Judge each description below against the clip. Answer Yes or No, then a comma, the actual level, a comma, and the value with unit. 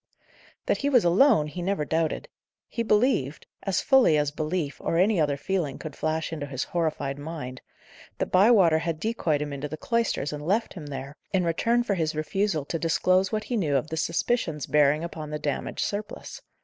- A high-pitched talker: No, medium, 160 Hz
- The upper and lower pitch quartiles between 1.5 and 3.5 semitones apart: No, average, 4.8 semitones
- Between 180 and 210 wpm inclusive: Yes, average, 190 wpm